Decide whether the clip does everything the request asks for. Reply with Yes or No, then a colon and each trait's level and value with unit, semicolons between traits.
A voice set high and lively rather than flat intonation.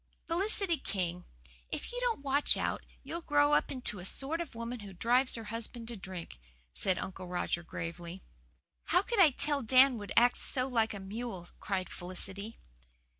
Yes: high, 230 Hz; wide, 7.1 semitones